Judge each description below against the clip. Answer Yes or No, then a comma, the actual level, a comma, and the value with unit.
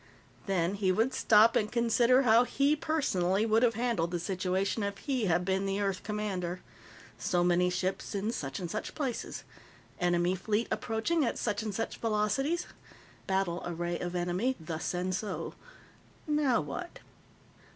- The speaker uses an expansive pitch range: No, average, 4.4 semitones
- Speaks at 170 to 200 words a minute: No, average, 155 wpm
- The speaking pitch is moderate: No, high, 200 Hz